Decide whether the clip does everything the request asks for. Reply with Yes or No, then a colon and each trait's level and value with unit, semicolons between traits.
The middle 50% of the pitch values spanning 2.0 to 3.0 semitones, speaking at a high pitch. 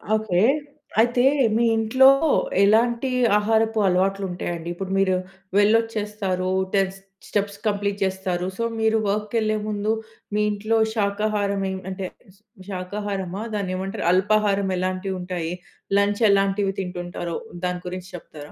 Yes: narrow, 2.5 semitones; high, 200 Hz